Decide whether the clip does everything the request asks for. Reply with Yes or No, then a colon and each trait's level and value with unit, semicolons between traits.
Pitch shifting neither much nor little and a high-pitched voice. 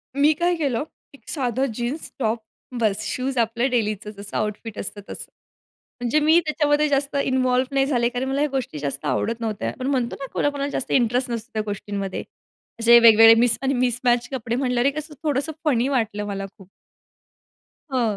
Yes: average, 3.6 semitones; high, 245 Hz